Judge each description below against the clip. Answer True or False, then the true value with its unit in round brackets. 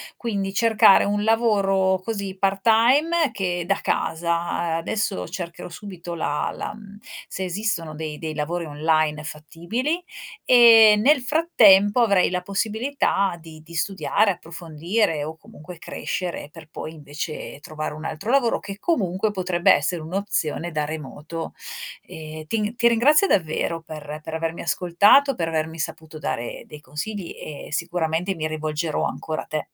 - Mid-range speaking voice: True (175 Hz)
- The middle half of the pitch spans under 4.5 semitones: False (4.8 semitones)